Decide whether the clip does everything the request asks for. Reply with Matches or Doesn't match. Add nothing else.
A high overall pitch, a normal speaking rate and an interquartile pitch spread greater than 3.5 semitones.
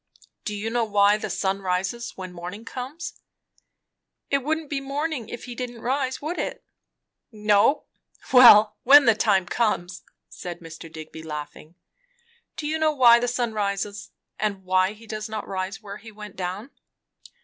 Matches